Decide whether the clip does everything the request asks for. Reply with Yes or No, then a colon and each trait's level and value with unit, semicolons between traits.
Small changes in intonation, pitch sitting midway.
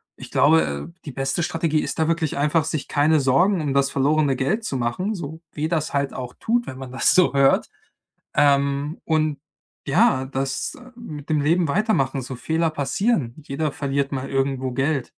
No: average, 3.0 semitones; medium, 145 Hz